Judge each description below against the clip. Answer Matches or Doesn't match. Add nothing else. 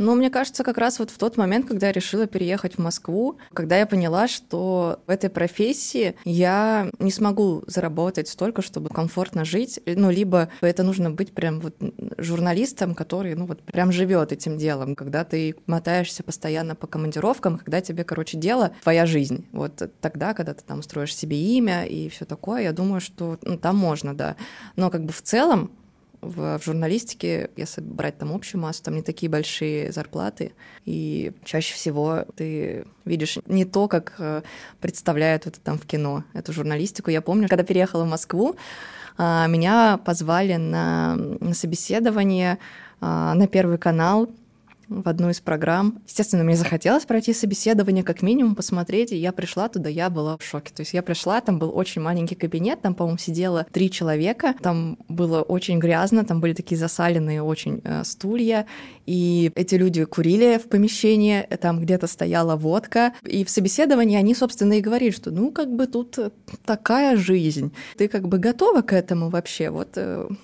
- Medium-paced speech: Doesn't match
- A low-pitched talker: Doesn't match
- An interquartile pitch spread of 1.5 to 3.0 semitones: Doesn't match